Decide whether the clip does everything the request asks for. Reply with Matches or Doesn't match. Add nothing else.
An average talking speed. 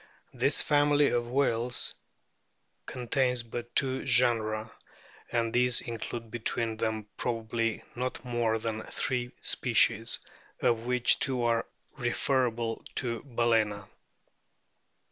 Doesn't match